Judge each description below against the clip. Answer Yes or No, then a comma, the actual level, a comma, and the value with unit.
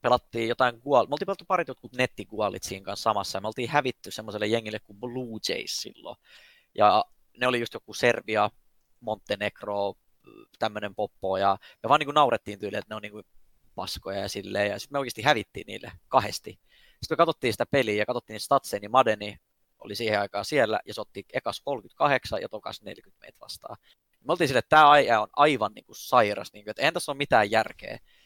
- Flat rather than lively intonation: No, average, 3.7 semitones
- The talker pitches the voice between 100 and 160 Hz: Yes, low, 110 Hz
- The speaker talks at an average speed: No, fast, 200 wpm